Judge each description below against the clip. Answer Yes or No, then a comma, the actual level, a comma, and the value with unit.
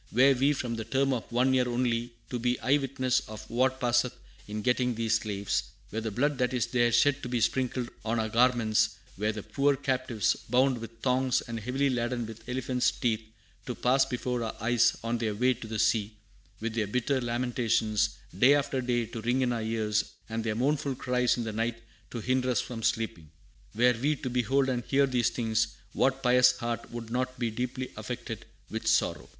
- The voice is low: Yes, low, 120 Hz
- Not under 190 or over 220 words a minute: Yes, average, 200 wpm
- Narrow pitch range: Yes, narrow, 2.2 semitones